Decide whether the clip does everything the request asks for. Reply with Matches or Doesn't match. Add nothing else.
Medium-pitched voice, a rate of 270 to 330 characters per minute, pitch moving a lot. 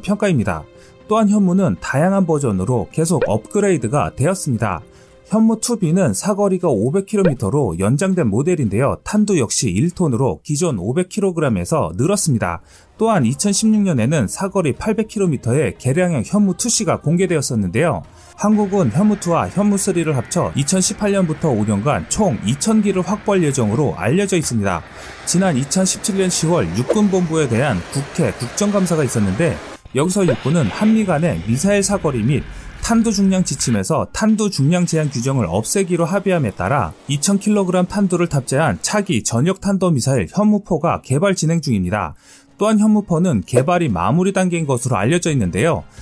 Matches